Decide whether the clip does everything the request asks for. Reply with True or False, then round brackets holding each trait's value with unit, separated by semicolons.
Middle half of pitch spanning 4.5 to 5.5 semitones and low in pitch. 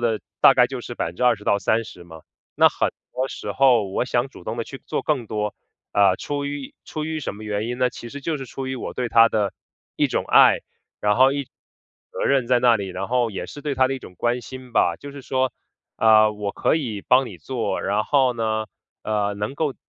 False (3.9 semitones; 120 Hz)